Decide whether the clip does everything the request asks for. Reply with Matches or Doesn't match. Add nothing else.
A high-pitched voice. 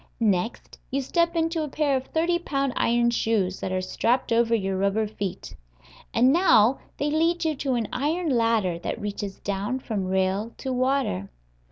Matches